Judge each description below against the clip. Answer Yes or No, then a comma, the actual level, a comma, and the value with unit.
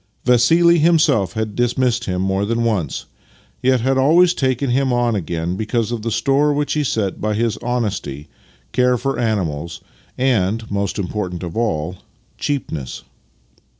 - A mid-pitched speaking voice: No, low, 115 Hz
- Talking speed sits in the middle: Yes, average, 150 wpm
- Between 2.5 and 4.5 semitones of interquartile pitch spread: No, average, 5.2 semitones